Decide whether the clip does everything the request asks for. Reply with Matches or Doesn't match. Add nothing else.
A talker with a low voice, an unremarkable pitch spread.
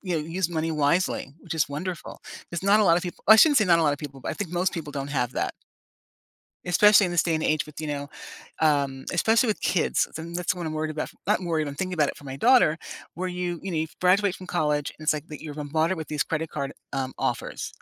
Doesn't match